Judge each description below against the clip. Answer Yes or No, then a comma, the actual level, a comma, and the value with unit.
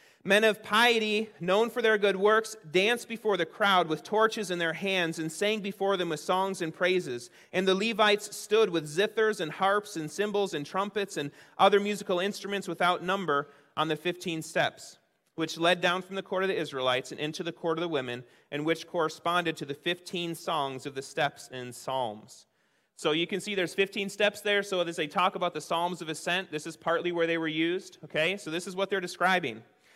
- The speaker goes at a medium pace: No, fast, 210 wpm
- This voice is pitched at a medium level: Yes, medium, 180 Hz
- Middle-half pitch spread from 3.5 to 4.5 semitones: Yes, average, 3.8 semitones